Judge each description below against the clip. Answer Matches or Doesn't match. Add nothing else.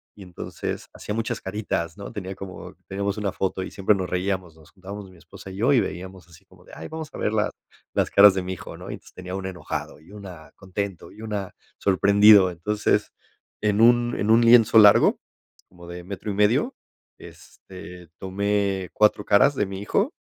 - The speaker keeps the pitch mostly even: Matches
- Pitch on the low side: Matches